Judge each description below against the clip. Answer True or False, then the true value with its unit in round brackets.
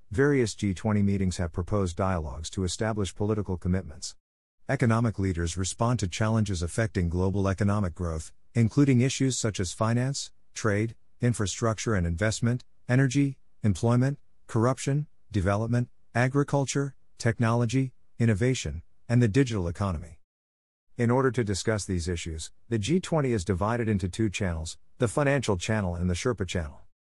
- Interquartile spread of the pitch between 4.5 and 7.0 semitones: True (4.9 semitones)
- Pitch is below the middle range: True (105 Hz)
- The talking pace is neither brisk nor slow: False (130 wpm)